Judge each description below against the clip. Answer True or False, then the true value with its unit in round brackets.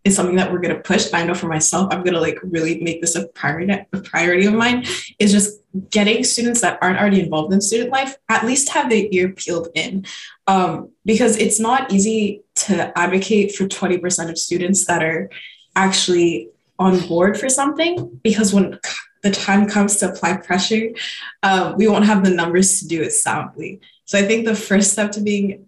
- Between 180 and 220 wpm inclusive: True (195 wpm)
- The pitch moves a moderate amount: True (3.2 semitones)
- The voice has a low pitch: False (195 Hz)